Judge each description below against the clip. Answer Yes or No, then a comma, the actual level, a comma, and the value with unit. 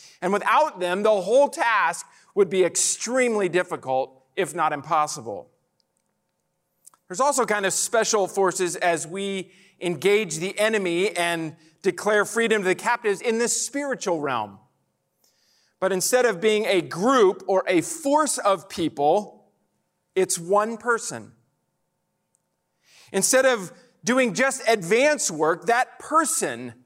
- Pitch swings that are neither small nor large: Yes, average, 4.9 semitones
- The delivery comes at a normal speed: No, slow, 125 wpm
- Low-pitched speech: No, high, 190 Hz